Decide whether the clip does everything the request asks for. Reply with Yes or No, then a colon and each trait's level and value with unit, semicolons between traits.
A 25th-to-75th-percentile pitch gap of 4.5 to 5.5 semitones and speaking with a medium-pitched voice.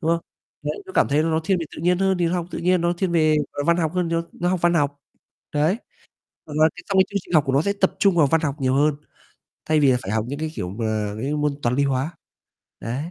No: average, 3.8 semitones; medium, 160 Hz